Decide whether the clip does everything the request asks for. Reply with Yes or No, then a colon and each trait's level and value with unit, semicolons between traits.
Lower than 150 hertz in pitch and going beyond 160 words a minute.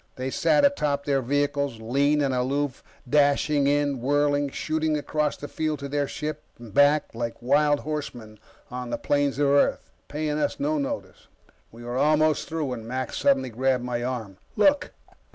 Yes: medium, 140 Hz; average, 170 wpm